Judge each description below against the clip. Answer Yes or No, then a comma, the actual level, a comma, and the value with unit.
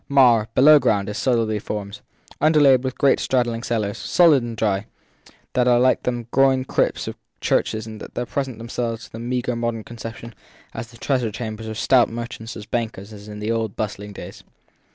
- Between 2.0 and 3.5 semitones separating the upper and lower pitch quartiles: Yes, narrow, 2.5 semitones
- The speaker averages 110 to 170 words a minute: No, average, 180 wpm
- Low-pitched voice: Yes, low, 115 Hz